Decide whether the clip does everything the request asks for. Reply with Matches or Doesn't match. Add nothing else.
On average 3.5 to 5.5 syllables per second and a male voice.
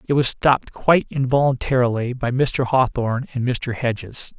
Matches